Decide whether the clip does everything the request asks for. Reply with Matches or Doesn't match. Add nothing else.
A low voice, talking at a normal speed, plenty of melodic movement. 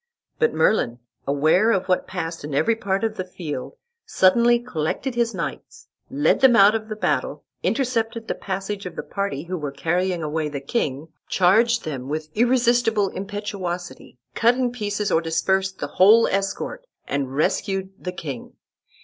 Doesn't match